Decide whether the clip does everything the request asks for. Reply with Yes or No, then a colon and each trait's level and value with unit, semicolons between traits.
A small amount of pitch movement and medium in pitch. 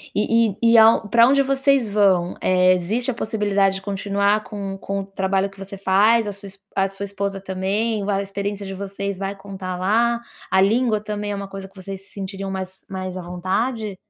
No: narrow, 1.7 semitones; high, 200 Hz